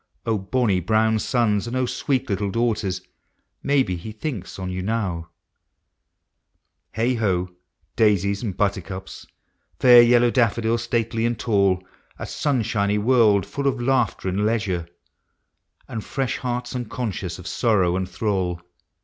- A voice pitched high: No, low, 110 Hz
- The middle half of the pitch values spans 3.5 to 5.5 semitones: Yes, average, 3.9 semitones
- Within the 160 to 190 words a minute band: No, slow, 135 wpm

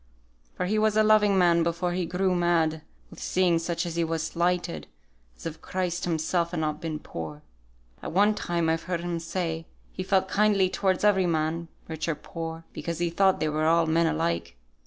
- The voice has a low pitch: No, medium, 170 Hz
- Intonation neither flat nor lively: No, narrow, 2.2 semitones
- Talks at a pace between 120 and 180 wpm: No, average, 200 wpm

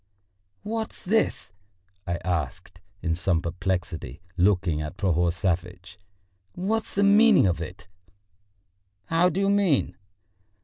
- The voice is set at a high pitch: No, very low, 95 Hz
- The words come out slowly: Yes, slow, 115 wpm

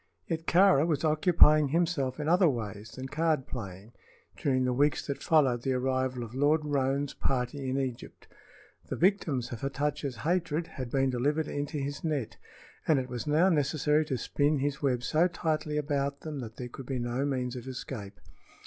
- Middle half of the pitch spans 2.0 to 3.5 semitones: Yes, average, 3.2 semitones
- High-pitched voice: No, medium, 140 Hz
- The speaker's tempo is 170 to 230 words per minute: Yes, average, 180 wpm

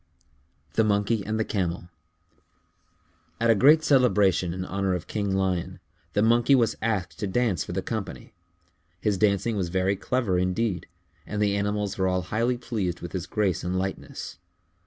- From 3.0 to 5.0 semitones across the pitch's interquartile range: Yes, average, 3.3 semitones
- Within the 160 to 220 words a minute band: Yes, average, 170 wpm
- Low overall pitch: Yes, low, 100 Hz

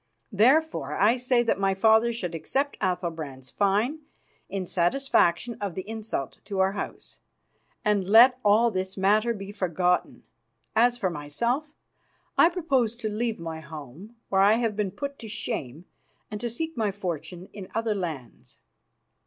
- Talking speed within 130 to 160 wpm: Yes, average, 155 wpm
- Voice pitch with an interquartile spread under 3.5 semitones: No, average, 4.6 semitones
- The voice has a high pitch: Yes, high, 205 Hz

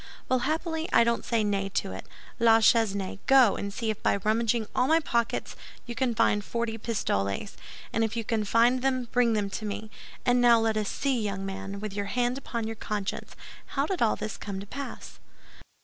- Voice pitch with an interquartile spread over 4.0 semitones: No, average, 2.9 semitones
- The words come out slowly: No, fast, 205 wpm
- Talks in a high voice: Yes, high, 225 Hz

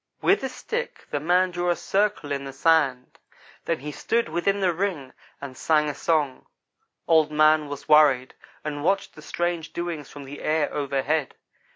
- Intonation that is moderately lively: Yes, average, 3.4 semitones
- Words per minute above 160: Yes, average, 175 wpm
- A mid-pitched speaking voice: Yes, medium, 155 Hz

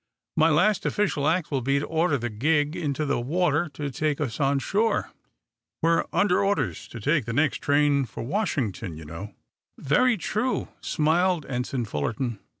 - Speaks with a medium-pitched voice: Yes, medium, 145 Hz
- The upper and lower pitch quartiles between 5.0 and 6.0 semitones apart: Yes, wide, 5.4 semitones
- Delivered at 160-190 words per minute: Yes, average, 165 wpm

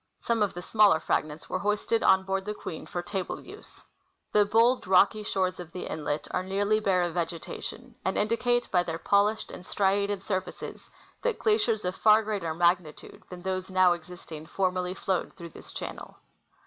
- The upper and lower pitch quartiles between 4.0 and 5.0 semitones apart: No, average, 3.0 semitones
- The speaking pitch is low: No, high, 190 Hz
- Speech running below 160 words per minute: No, average, 175 wpm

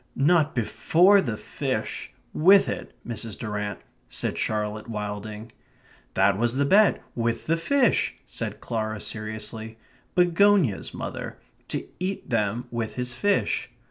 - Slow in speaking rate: Yes, slow, 125 wpm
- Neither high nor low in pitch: No, low, 115 Hz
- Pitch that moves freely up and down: Yes, wide, 7.5 semitones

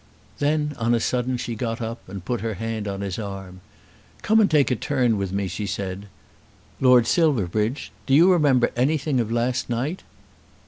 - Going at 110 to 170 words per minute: No, average, 180 wpm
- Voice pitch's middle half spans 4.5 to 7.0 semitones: Yes, average, 5.0 semitones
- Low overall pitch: Yes, low, 120 Hz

